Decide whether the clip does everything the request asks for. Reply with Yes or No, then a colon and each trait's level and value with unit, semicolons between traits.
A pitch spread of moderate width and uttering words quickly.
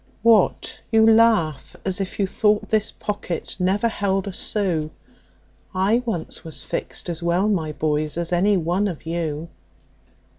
No: average, 3.9 semitones; average, 150 wpm